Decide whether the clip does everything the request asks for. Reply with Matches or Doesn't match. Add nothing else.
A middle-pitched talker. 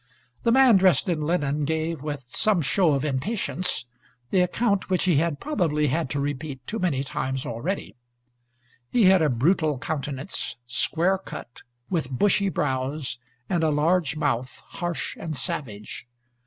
Matches